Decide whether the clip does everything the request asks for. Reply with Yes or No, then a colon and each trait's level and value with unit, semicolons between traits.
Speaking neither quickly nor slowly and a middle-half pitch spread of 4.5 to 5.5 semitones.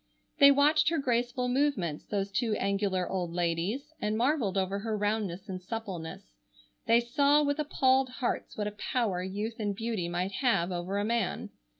Yes: average, 170 wpm; average, 4.9 semitones